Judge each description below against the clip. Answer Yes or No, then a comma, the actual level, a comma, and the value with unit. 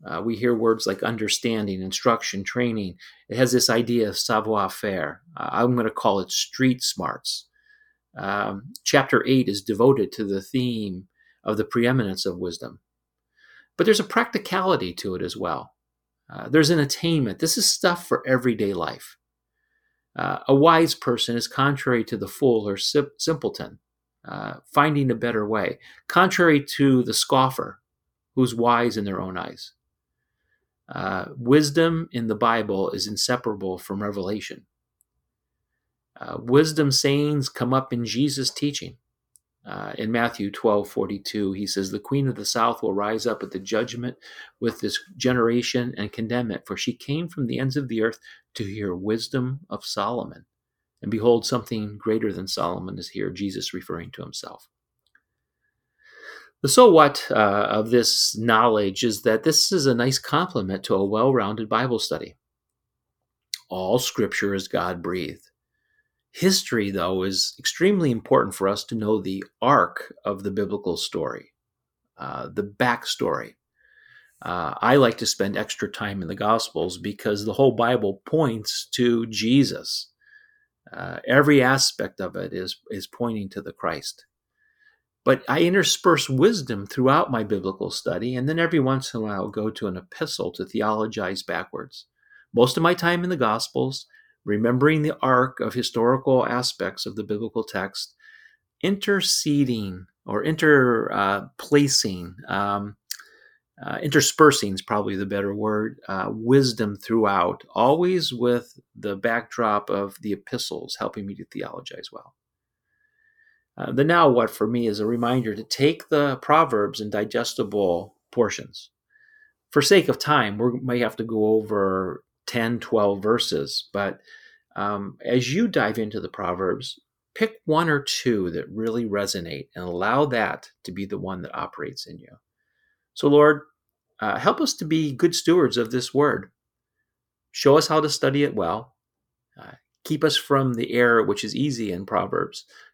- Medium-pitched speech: No, low, 120 Hz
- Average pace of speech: Yes, average, 155 wpm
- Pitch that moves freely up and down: Yes, wide, 5.8 semitones